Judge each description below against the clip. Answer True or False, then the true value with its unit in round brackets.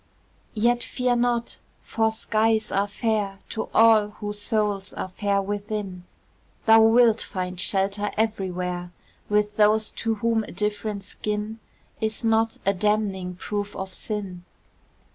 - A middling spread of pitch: False (2.0 semitones)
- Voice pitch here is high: True (210 Hz)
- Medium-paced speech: False (130 wpm)